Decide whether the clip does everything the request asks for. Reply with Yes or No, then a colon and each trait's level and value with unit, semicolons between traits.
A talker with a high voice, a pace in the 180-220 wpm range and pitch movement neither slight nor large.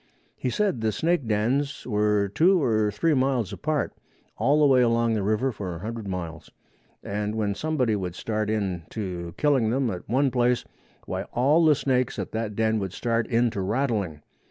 No: low, 115 Hz; average, 185 wpm; average, 4.3 semitones